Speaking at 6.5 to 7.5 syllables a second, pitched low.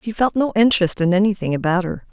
No: 6.6 syllables/s; high, 195 Hz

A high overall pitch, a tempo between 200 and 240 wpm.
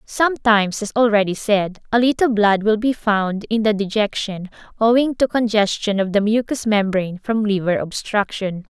No: high, 215 Hz; average, 160 wpm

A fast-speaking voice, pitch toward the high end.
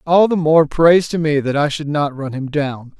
No: fast, 260 wpm; medium, 150 Hz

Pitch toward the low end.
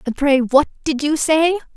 No: very high, 290 Hz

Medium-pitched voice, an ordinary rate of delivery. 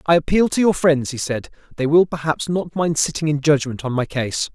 No: medium, 155 Hz; fast, 235 wpm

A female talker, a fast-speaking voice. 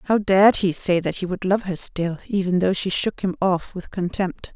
Yes: female; fast, 235 wpm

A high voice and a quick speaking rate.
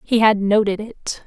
No: high, 210 Hz; average, 190 wpm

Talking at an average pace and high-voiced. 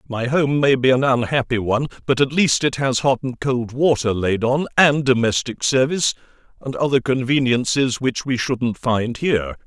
No: average, 180 wpm; low, 130 Hz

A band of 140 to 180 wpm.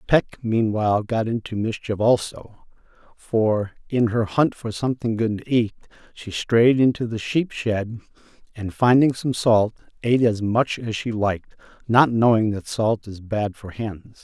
Yes: average, 165 wpm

